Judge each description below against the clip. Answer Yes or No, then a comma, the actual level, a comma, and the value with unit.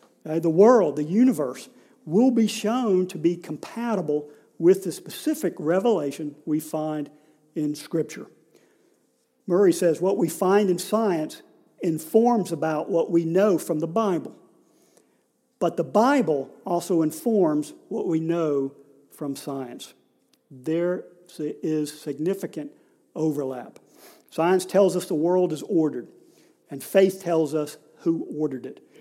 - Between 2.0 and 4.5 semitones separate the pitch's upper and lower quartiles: Yes, average, 4.1 semitones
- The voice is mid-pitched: Yes, medium, 170 Hz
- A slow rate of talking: Yes, slow, 130 wpm